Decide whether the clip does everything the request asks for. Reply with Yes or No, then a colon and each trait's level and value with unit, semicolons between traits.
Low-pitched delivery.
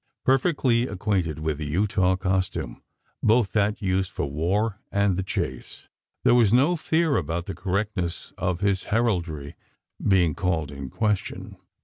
Yes: very low, 95 Hz